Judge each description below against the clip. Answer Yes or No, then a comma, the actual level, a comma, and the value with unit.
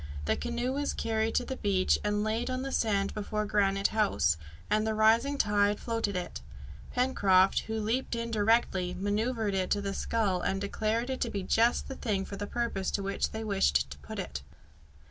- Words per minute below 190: No, average, 195 wpm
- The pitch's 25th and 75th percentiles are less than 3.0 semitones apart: Yes, narrow, 2.6 semitones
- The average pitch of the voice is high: Yes, high, 210 Hz